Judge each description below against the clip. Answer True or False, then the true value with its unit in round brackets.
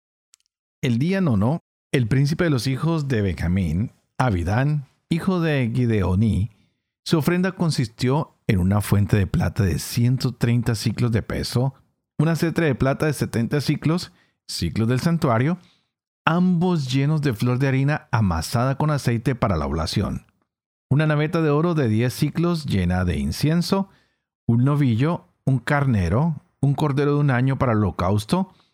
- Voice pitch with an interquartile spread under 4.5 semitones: False (5.6 semitones)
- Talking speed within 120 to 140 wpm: False (150 wpm)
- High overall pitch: False (135 Hz)